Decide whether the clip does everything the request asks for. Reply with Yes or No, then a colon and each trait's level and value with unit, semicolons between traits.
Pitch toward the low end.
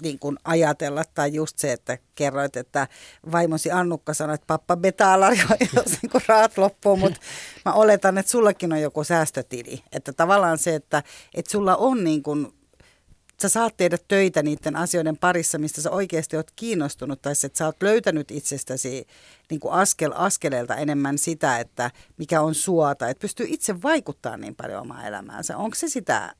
No: medium, 165 Hz